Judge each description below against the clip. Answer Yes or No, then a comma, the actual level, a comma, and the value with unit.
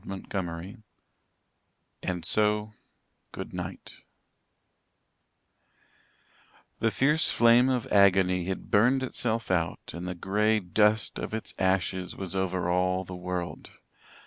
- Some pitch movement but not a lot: Yes, average, 3.1 semitones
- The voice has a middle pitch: No, very low, 95 Hz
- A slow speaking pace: Yes, slow, 110 wpm